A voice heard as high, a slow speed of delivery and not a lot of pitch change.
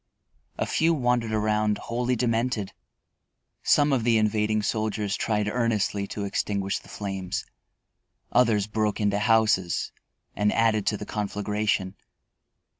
No: low, 105 Hz; slow, 120 wpm; narrow, 1.9 semitones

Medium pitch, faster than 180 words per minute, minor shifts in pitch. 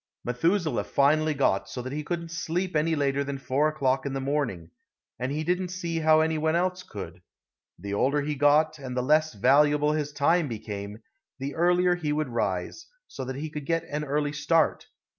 No: medium, 150 Hz; average, 195 wpm; average, 3.1 semitones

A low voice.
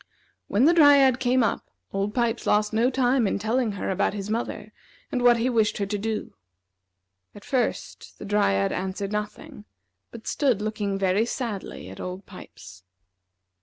No: high, 215 Hz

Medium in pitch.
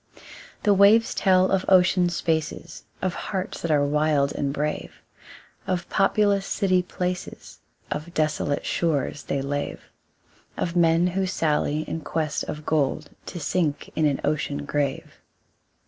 Yes: medium, 165 Hz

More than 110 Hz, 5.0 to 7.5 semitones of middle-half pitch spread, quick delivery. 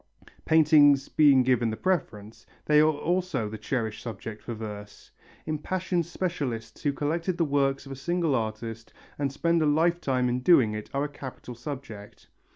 No: medium, 140 Hz; wide, 5.6 semitones; average, 165 wpm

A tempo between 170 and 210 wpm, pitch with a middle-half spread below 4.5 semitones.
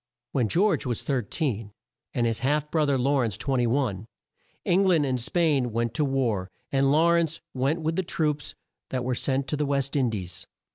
Yes: average, 190 wpm; average, 4.0 semitones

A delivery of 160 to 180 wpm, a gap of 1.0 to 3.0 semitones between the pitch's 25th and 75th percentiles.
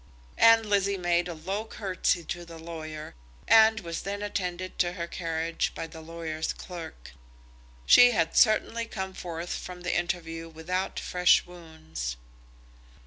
No: average, 140 wpm; average, 2.7 semitones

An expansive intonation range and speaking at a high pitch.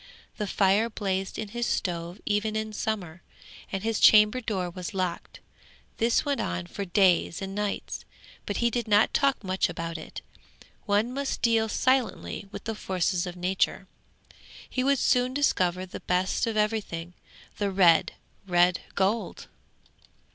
No: average, 3.6 semitones; high, 200 Hz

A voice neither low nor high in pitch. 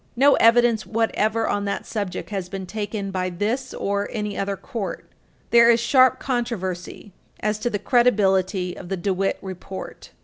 No: high, 205 Hz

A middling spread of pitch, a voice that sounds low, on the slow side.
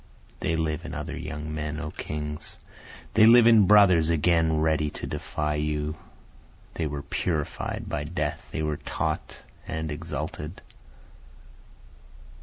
No: narrow, 1.6 semitones; very low, 80 Hz; slow, 130 wpm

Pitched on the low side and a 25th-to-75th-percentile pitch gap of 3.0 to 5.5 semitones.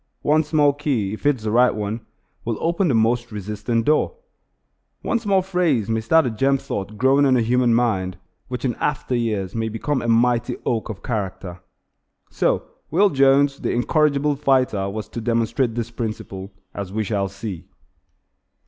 Yes: low, 120 Hz; average, 4.4 semitones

